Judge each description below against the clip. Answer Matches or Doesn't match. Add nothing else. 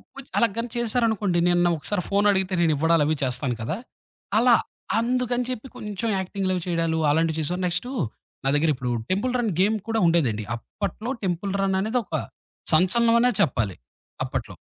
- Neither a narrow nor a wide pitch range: Doesn't match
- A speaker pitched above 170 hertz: Matches